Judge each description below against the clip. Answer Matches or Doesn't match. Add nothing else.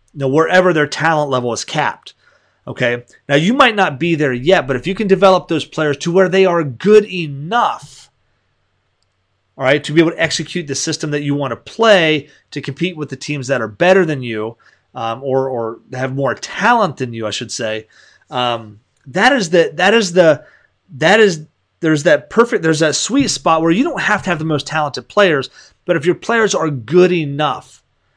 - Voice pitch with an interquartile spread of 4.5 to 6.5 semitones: Matches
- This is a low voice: Doesn't match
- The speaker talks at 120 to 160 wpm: Doesn't match